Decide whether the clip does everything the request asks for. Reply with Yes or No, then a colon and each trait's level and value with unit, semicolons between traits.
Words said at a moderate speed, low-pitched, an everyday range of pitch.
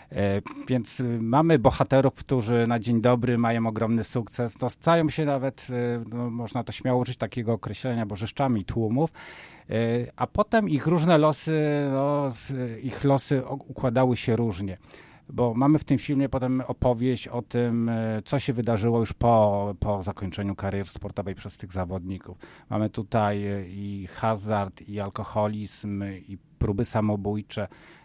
Yes: average, 135 wpm; low, 115 Hz; average, 4.0 semitones